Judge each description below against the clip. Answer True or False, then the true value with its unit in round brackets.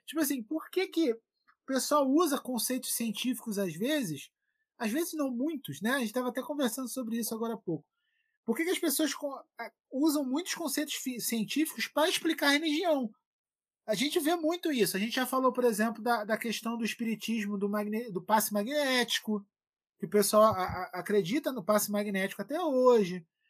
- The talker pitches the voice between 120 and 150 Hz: False (250 Hz)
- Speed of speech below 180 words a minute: False (185 wpm)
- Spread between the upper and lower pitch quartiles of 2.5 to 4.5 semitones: False (5.6 semitones)